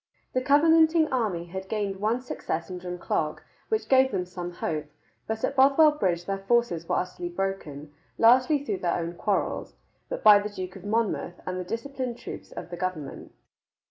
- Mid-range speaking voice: No, high, 195 Hz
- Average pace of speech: Yes, average, 175 wpm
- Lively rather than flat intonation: Yes, wide, 6.3 semitones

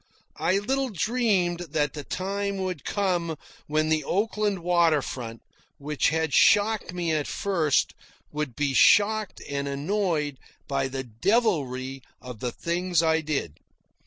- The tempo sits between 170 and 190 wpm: No, slow, 135 wpm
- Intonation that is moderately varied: No, wide, 5.7 semitones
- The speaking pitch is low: No, medium, 160 Hz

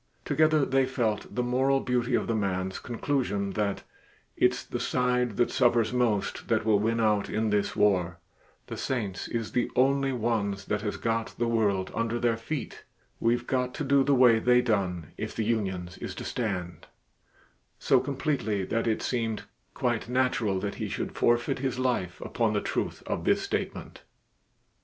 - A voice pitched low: Yes, low, 115 Hz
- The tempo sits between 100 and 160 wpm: No, average, 170 wpm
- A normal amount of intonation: Yes, average, 3.4 semitones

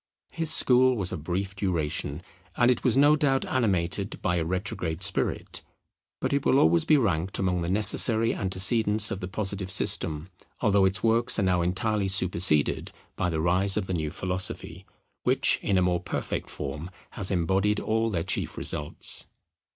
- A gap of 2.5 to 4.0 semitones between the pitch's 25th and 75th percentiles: Yes, average, 3.6 semitones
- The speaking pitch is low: Yes, very low, 95 Hz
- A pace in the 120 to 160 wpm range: No, average, 170 wpm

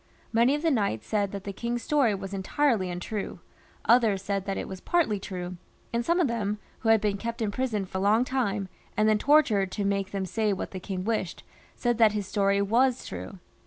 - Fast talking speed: Yes, fast, 215 wpm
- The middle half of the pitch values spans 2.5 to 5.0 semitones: Yes, average, 3.1 semitones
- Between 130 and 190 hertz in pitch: No, high, 210 Hz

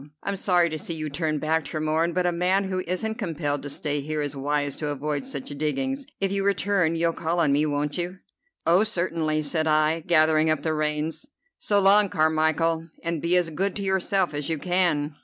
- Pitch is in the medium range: Yes, medium, 160 Hz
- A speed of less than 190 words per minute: No, fast, 205 wpm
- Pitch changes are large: No, average, 3.0 semitones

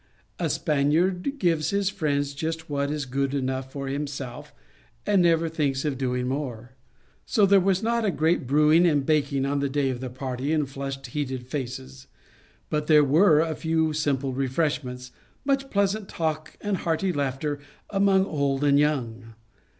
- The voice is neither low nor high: Yes, medium, 145 Hz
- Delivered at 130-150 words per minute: No, average, 165 wpm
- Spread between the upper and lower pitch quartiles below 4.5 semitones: Yes, average, 3.4 semitones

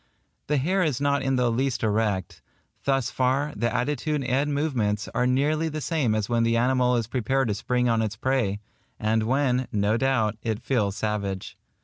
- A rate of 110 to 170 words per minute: No, average, 185 wpm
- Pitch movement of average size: Yes, average, 3.8 semitones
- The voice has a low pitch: Yes, low, 125 Hz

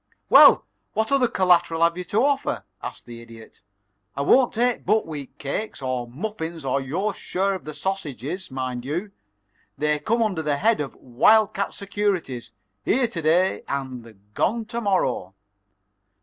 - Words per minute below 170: Yes, average, 155 wpm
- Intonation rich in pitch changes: Yes, wide, 7.7 semitones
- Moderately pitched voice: Yes, medium, 170 Hz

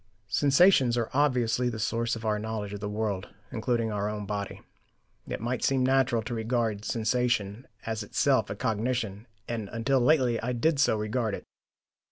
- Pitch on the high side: No, low, 115 Hz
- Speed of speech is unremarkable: Yes, average, 175 wpm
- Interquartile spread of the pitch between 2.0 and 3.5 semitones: Yes, average, 2.8 semitones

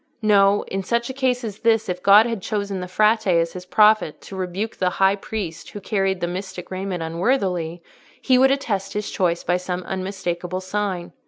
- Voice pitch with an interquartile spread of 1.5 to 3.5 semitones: Yes, average, 2.8 semitones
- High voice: Yes, high, 195 Hz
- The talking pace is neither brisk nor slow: Yes, average, 190 wpm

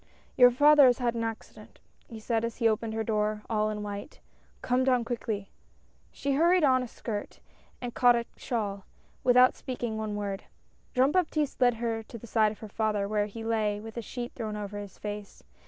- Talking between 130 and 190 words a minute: No, fast, 205 wpm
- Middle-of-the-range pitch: No, high, 225 Hz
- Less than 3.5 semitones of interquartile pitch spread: Yes, average, 2.7 semitones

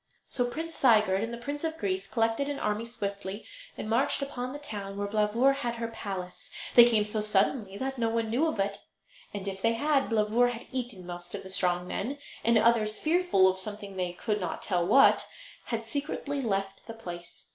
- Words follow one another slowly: No, average, 200 wpm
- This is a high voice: Yes, high, 225 Hz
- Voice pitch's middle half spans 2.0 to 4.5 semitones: Yes, average, 3.8 semitones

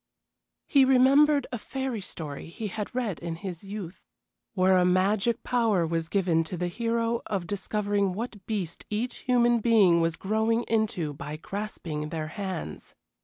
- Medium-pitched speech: No, high, 200 Hz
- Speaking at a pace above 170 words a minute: No, average, 155 wpm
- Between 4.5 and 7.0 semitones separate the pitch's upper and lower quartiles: Yes, average, 5.1 semitones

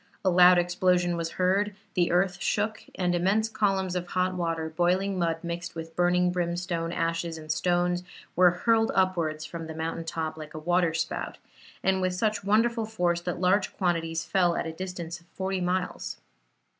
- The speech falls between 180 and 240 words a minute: No, average, 170 wpm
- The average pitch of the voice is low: No, medium, 180 Hz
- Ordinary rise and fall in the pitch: No, narrow, 2.0 semitones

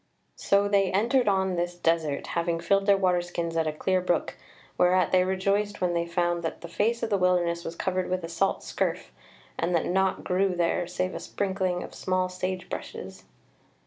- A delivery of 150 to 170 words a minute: No, average, 195 wpm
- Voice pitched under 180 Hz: No, medium, 185 Hz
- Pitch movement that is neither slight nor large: No, narrow, 1.9 semitones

